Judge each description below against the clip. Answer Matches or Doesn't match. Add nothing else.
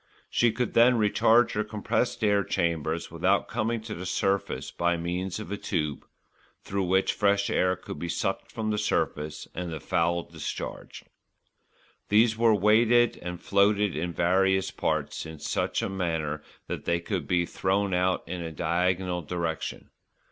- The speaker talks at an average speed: Matches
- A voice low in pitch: Matches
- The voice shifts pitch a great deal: Doesn't match